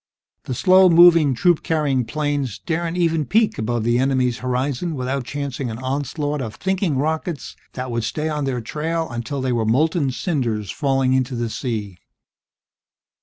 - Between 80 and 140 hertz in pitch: Yes, low, 135 Hz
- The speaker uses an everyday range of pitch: Yes, average, 4.4 semitones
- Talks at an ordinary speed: Yes, average, 160 wpm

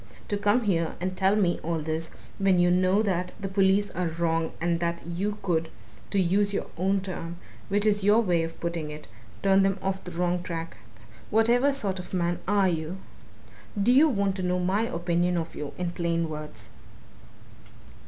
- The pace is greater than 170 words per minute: Yes, average, 185 wpm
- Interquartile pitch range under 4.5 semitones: Yes, average, 2.8 semitones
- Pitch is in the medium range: Yes, medium, 180 Hz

